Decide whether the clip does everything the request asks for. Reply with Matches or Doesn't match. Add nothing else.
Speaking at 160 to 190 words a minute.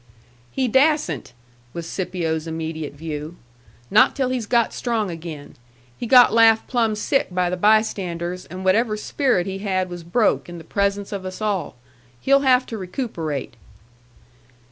Doesn't match